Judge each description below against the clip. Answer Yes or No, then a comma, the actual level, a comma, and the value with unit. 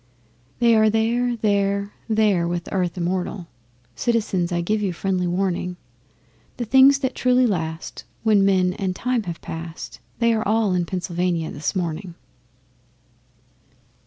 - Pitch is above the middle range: Yes, high, 195 Hz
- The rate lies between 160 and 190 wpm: No, slow, 135 wpm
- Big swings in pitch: No, average, 4.0 semitones